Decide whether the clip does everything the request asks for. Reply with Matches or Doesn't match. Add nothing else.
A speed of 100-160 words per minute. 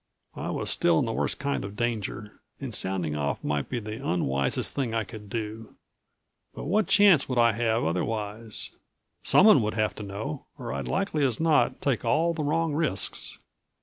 Doesn't match